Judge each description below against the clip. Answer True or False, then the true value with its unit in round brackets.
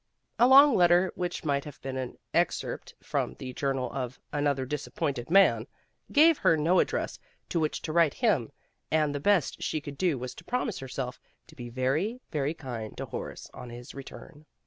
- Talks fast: False (190 wpm)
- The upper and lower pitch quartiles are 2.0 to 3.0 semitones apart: False (5.2 semitones)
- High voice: False (145 Hz)